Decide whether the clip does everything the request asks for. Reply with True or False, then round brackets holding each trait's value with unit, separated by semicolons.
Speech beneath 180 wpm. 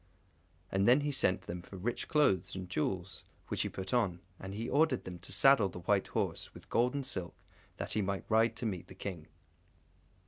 False (205 wpm)